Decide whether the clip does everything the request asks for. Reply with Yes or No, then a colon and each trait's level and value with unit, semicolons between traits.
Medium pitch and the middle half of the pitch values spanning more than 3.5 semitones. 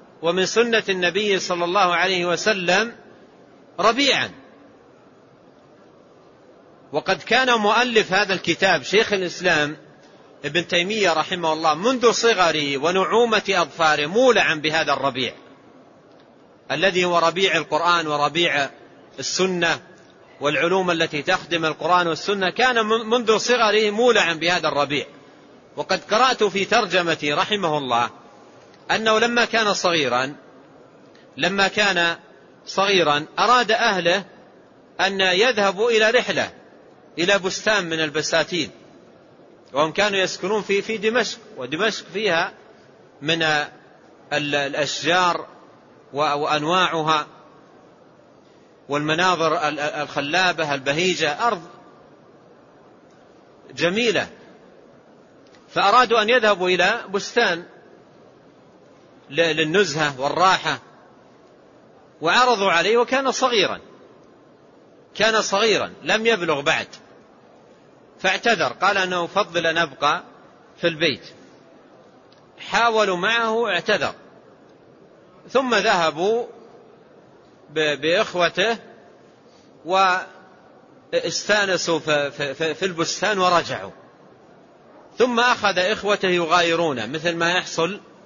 Yes: medium, 180 Hz; average, 5.1 semitones